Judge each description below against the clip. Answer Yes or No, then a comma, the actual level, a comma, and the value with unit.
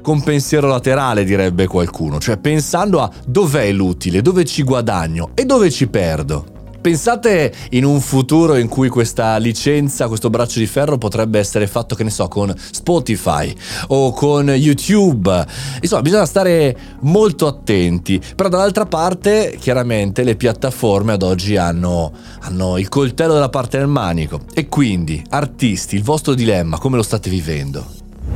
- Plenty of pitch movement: Yes, wide, 7.1 semitones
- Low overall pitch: Yes, low, 120 Hz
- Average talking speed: Yes, average, 150 wpm